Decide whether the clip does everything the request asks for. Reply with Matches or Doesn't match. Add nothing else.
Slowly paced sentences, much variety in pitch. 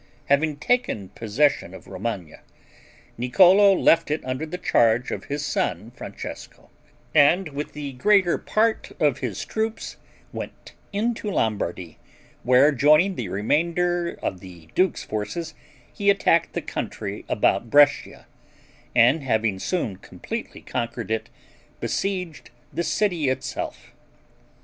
Matches